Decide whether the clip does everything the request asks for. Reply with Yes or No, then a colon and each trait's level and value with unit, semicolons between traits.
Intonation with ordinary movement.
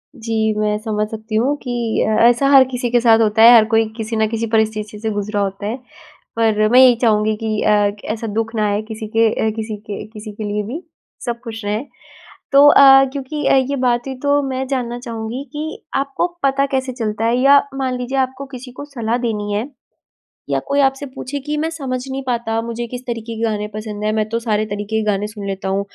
Yes: average, 3.3 semitones